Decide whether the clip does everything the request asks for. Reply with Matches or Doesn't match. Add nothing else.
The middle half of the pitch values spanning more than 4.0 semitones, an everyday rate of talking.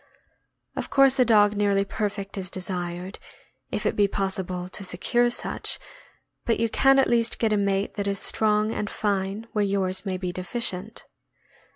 Doesn't match